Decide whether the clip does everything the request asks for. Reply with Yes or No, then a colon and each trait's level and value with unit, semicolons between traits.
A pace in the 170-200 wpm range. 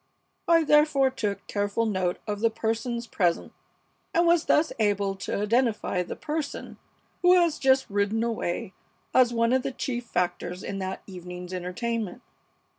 No: average, 150 wpm